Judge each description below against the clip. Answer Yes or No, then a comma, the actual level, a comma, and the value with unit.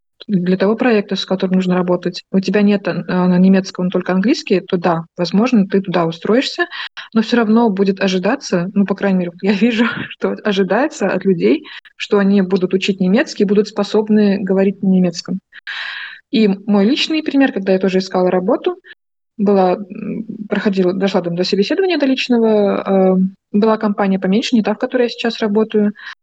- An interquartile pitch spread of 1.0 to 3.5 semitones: Yes, average, 2.8 semitones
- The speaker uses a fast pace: Yes, fast, 165 wpm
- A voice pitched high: Yes, high, 200 Hz